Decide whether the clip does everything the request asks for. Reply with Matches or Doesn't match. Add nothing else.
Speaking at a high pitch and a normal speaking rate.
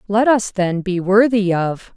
Matches